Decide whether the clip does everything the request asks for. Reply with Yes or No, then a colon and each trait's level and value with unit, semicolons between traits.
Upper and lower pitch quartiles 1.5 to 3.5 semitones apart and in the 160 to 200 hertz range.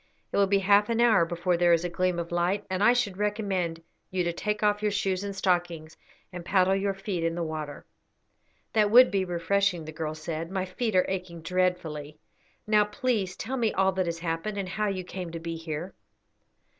Yes: average, 3.2 semitones; medium, 185 Hz